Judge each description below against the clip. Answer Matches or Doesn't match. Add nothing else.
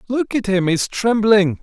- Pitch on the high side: Matches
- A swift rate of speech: Doesn't match